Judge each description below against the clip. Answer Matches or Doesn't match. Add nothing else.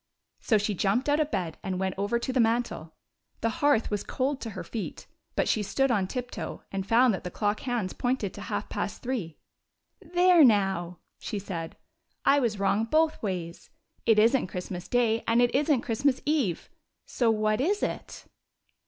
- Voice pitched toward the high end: Matches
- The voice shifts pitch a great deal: Doesn't match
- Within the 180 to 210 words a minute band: Matches